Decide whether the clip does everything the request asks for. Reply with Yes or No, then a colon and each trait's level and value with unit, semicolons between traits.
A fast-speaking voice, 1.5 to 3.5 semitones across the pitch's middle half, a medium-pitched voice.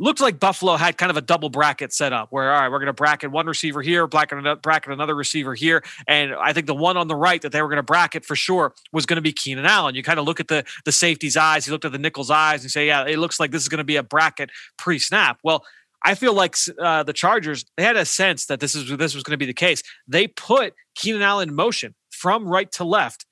Yes: fast, 275 wpm; narrow, 2.6 semitones; medium, 155 Hz